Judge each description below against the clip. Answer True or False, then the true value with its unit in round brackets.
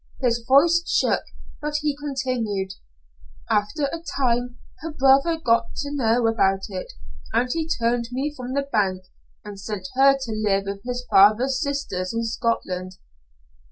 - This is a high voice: True (240 Hz)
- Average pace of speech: True (150 wpm)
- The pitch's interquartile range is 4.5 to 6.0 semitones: True (4.9 semitones)